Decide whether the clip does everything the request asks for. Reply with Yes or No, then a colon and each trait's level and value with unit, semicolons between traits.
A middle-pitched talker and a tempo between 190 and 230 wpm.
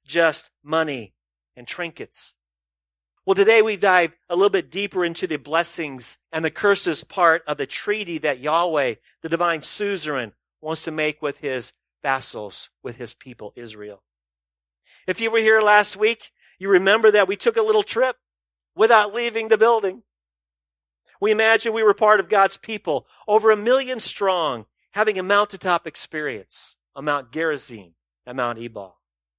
No: medium, 165 Hz; average, 155 wpm